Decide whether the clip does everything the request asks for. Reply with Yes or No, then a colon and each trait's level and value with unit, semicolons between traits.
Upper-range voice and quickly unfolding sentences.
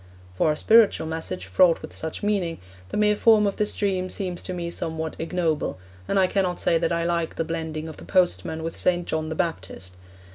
No: medium, 170 Hz; fast, 210 wpm